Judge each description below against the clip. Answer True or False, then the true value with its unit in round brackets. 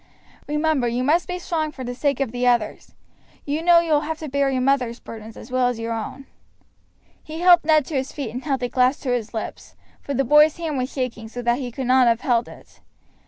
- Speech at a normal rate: False (240 wpm)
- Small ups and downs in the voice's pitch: False (3.7 semitones)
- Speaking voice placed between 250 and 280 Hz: True (265 Hz)